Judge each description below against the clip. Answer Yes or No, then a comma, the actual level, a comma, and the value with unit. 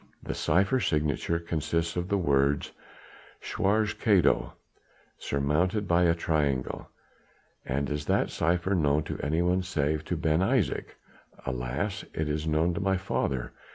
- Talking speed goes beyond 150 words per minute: No, slow, 135 wpm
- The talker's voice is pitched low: Yes, very low, 85 Hz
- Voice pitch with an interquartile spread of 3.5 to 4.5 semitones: Yes, average, 3.8 semitones